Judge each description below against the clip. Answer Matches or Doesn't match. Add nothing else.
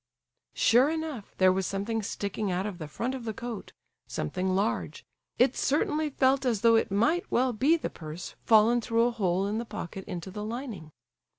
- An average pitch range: Matches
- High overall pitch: Matches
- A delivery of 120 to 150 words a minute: Doesn't match